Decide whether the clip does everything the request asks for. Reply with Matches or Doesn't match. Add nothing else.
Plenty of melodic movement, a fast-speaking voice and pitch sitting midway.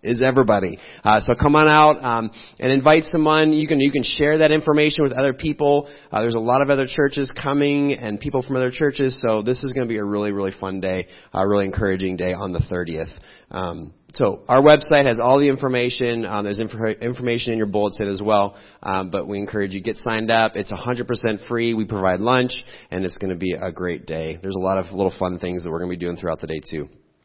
Doesn't match